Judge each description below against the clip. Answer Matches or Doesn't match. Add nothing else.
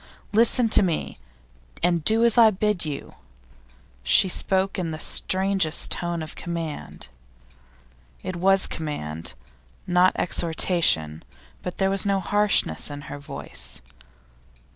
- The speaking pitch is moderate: Matches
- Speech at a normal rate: Doesn't match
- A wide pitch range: Doesn't match